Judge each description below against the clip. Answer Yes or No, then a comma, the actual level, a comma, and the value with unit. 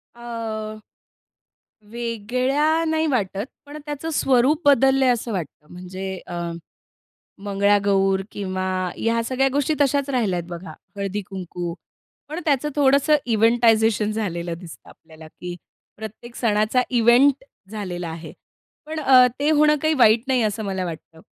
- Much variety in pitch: Yes, wide, 5.7 semitones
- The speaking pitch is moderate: No, high, 225 Hz